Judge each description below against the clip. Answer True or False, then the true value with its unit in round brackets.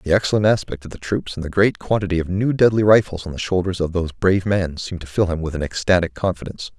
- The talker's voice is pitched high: False (90 Hz)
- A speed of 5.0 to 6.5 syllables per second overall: False (6.8 syllables/s)